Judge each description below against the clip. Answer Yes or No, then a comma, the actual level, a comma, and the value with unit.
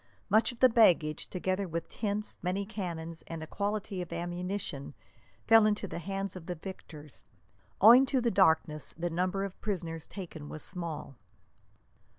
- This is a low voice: No, medium, 185 Hz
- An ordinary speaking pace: Yes, average, 160 wpm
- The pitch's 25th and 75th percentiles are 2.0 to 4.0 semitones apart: Yes, average, 3.7 semitones